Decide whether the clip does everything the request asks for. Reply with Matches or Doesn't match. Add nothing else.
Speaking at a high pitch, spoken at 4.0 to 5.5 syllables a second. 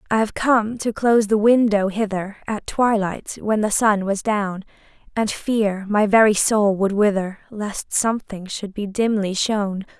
Matches